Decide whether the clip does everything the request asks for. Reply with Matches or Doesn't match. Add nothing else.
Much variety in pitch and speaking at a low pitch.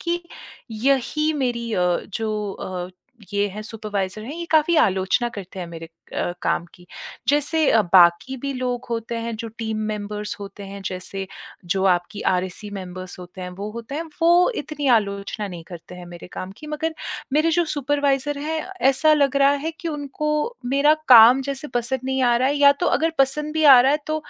Doesn't match